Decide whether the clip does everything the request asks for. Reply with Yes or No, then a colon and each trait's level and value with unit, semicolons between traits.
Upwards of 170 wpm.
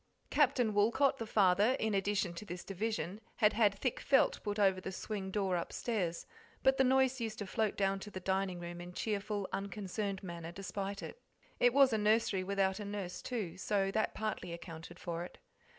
Yes: average, 190 wpm